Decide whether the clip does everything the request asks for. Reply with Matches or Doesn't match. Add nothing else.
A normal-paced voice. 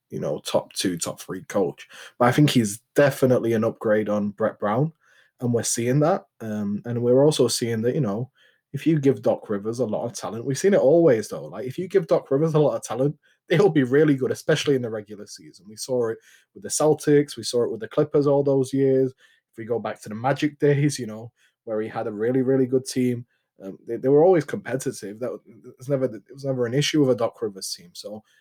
Doesn't match